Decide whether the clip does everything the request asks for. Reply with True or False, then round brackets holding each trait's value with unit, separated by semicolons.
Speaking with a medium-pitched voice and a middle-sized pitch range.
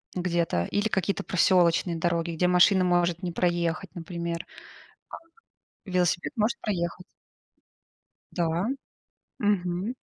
False (175 Hz; 1.5 semitones)